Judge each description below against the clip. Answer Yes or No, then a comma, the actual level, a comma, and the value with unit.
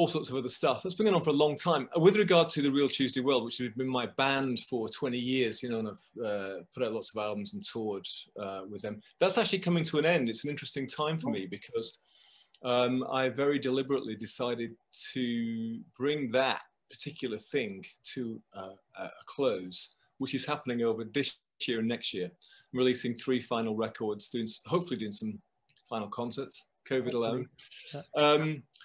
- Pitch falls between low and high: No, low, 130 Hz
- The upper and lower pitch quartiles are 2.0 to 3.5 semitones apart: No, average, 4.3 semitones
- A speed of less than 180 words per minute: No, average, 195 wpm